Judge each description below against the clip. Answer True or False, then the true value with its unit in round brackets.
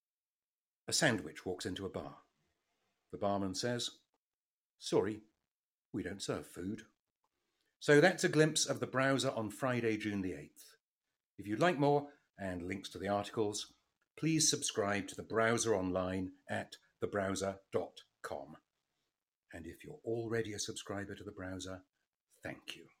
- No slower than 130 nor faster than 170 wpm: True (140 wpm)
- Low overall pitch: True (105 Hz)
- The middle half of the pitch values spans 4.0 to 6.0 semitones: True (4.9 semitones)